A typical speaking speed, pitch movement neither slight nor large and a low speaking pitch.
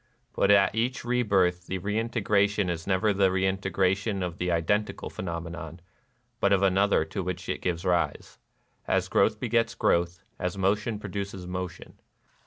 No: average, 150 wpm; narrow, 2.3 semitones; very low, 95 Hz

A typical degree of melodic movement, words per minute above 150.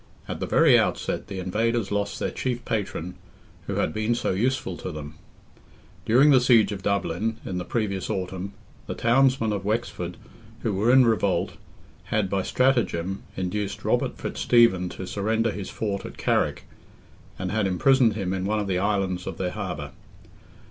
Yes: average, 3.5 semitones; average, 170 wpm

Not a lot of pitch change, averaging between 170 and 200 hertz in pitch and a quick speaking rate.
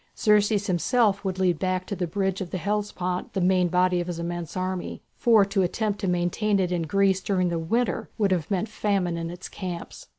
Yes: narrow, 2.3 semitones; medium, 185 Hz; fast, 210 wpm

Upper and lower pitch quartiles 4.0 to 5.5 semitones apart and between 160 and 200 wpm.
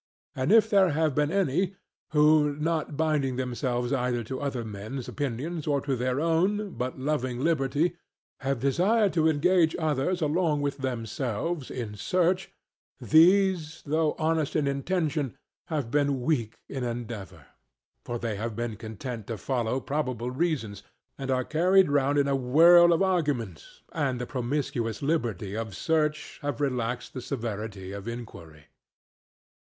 No: average, 4.8 semitones; average, 145 wpm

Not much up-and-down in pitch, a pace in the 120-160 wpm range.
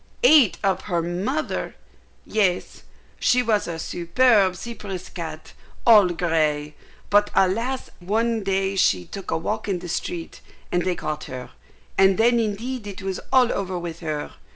No: average, 4.4 semitones; average, 155 wpm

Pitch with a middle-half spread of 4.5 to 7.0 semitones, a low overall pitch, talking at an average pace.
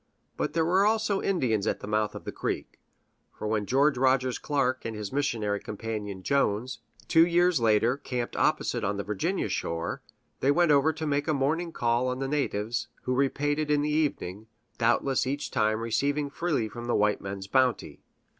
Yes: average, 5.3 semitones; low, 130 Hz; average, 185 wpm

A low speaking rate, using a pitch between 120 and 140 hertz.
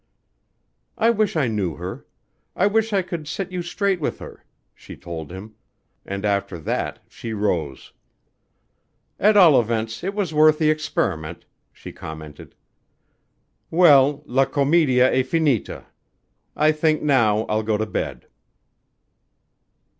Yes: slow, 130 wpm; low, 135 Hz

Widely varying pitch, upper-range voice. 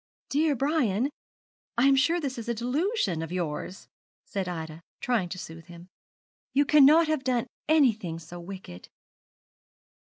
Yes: wide, 8.3 semitones; high, 235 Hz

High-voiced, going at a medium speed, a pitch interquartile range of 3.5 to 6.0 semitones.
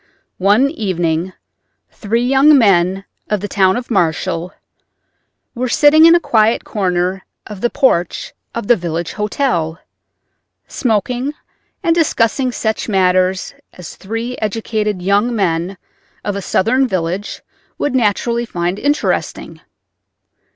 No: high, 210 Hz; slow, 120 wpm; average, 4.9 semitones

